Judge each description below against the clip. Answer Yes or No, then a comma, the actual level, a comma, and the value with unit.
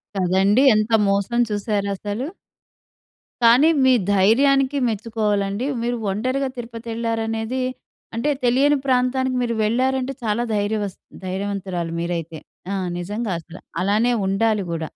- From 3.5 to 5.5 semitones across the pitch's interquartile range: Yes, average, 3.8 semitones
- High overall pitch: Yes, high, 220 Hz